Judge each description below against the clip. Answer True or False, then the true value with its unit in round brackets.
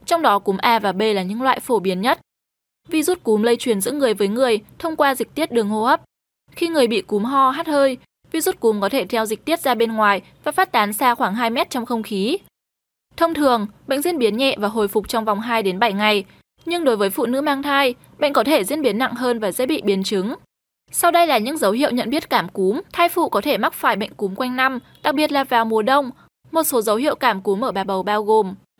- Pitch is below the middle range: False (245 Hz)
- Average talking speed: False (260 wpm)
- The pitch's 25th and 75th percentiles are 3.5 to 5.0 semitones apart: False (5.4 semitones)